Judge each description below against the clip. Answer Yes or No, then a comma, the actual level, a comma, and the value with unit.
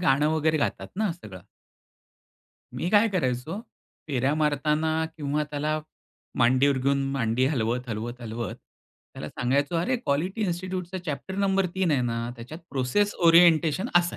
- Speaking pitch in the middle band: Yes, medium, 150 Hz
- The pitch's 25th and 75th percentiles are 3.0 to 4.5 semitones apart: No, wide, 5.6 semitones